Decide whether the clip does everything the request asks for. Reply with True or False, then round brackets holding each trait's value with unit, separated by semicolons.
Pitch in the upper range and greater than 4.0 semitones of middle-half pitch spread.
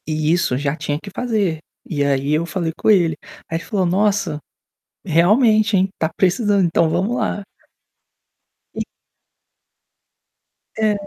False (175 Hz; 4.4 semitones)